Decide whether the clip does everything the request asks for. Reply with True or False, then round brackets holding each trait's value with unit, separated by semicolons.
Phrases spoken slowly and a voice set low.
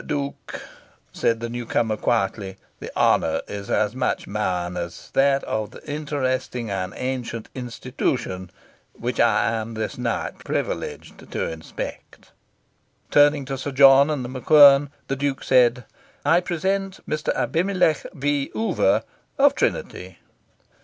True (130 wpm; 130 Hz)